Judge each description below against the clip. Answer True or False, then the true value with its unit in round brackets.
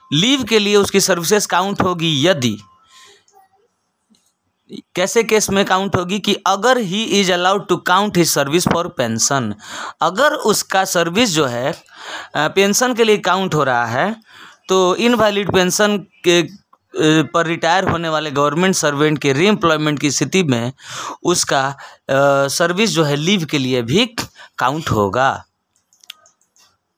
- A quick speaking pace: False (140 wpm)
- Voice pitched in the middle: True (180 Hz)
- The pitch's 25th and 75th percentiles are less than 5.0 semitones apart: False (5.5 semitones)